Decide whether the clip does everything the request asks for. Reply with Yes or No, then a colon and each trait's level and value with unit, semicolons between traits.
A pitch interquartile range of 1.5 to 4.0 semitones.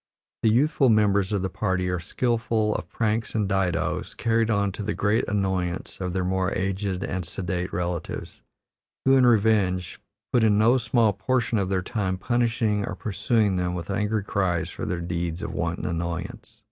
Yes: average, 3.5 semitones